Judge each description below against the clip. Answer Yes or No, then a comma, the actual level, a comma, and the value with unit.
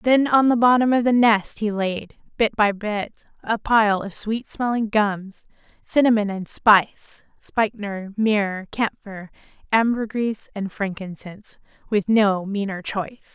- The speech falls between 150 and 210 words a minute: No, average, 140 wpm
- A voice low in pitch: No, high, 210 Hz